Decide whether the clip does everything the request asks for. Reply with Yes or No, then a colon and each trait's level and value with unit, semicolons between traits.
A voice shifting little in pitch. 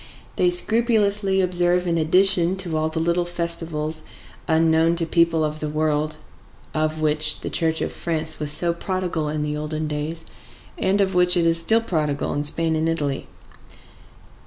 Yes: narrow, 2.3 semitones